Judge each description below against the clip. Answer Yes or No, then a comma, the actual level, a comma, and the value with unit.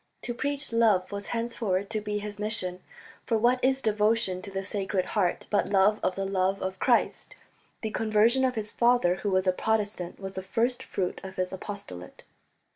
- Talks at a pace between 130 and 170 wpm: No, average, 190 wpm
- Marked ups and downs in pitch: No, average, 3.1 semitones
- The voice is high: Yes, high, 205 Hz